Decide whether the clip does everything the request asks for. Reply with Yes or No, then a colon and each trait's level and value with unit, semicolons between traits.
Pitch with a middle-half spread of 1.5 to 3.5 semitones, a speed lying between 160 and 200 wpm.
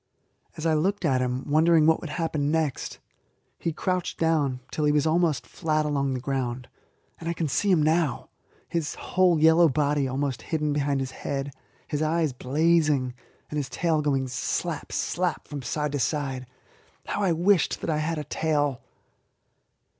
Yes: average, 2.8 semitones; average, 170 wpm